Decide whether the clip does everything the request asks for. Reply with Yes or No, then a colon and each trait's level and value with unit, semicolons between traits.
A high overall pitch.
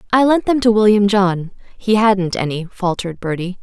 Yes: high, 200 Hz